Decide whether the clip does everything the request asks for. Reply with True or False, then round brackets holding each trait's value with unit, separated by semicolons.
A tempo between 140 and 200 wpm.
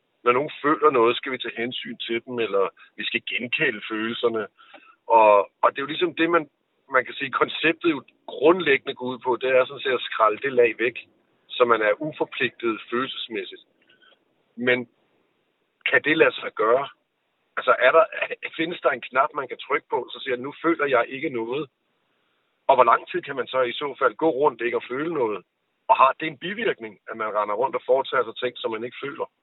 False (210 wpm)